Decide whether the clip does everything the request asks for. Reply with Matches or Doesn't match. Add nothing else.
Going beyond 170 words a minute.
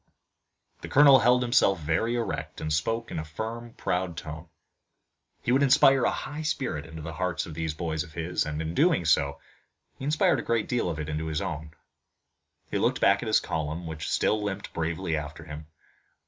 Matches